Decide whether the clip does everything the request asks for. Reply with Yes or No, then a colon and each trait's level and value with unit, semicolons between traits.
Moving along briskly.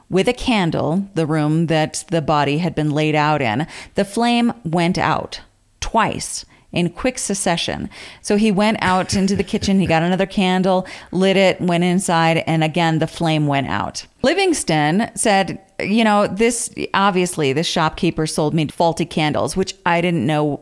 No: average, 170 wpm